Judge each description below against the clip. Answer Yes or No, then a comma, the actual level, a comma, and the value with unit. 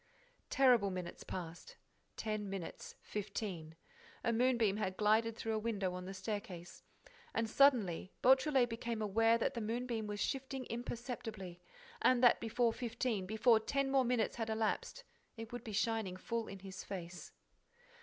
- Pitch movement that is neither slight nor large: Yes, average, 3.5 semitones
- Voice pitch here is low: No, high, 220 Hz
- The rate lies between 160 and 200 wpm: No, average, 150 wpm